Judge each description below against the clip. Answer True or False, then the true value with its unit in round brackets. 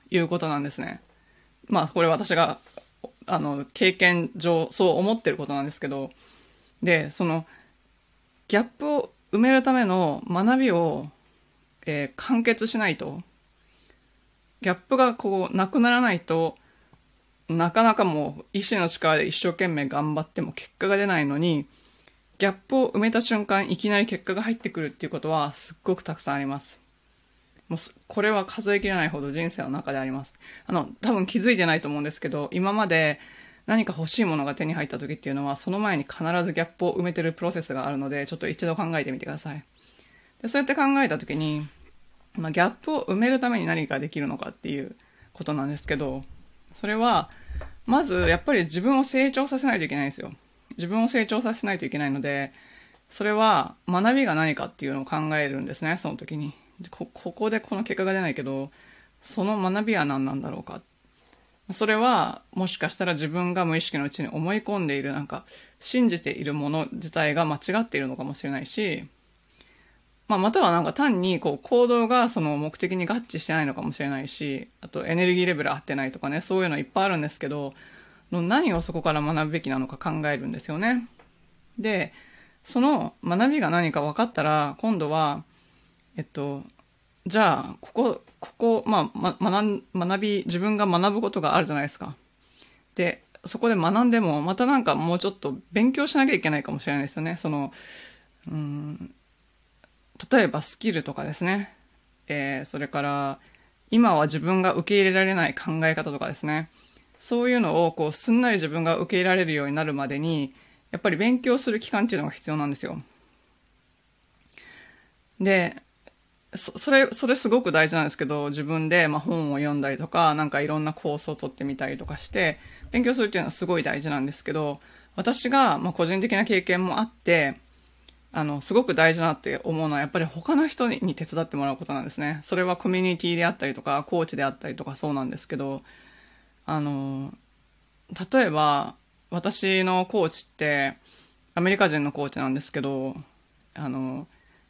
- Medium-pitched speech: True (170 Hz)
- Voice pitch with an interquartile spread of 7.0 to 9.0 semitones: False (6.0 semitones)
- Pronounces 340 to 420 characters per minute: True (370 characters per minute)